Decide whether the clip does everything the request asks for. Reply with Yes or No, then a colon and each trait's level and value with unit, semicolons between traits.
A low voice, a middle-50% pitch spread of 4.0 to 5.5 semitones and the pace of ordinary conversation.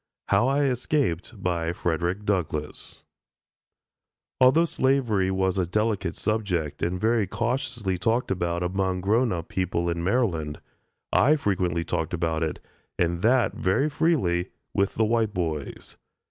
No: very low, 95 Hz; average, 5.2 semitones; slow, 130 wpm